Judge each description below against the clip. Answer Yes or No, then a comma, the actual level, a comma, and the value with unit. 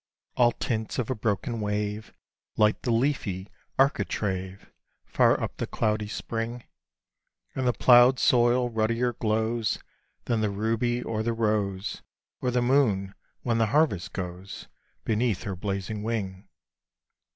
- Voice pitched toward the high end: No, low, 110 Hz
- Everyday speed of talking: No, slow, 130 wpm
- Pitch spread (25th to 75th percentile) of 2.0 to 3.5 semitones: Yes, average, 2.8 semitones